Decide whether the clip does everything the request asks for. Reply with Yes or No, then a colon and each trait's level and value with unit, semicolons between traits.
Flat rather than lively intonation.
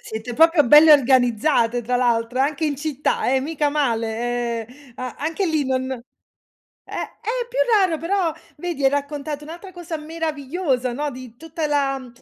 No: average, 4.3 semitones